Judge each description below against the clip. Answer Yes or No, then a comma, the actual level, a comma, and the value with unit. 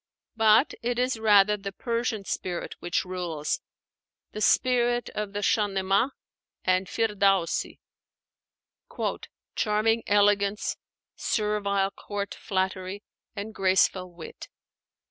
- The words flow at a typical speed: No, slow, 95 wpm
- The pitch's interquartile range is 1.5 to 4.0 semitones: Yes, narrow, 2.4 semitones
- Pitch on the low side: No, high, 205 Hz